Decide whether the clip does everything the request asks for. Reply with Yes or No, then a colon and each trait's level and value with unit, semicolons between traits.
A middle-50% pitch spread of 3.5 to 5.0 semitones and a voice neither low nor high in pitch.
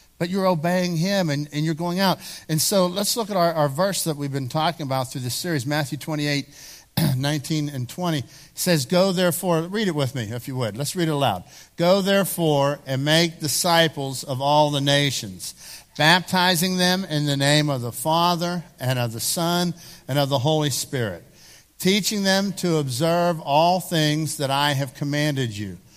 Yes: average, 3.9 semitones; medium, 155 Hz